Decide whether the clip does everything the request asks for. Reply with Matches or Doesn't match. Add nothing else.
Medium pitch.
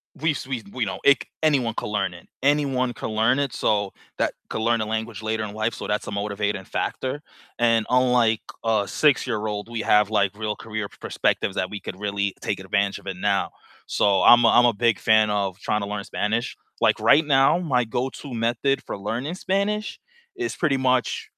Doesn't match